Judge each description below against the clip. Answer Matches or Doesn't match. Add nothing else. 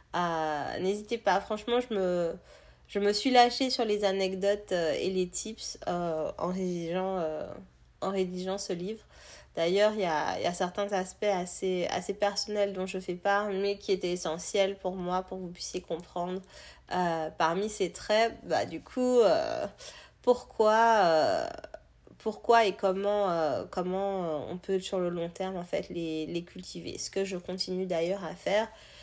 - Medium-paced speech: Matches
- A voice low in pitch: Doesn't match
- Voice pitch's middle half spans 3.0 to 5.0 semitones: Doesn't match